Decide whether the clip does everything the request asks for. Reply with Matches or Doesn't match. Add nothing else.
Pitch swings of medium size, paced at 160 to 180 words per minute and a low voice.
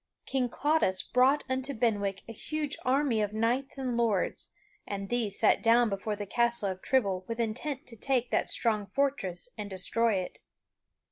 Doesn't match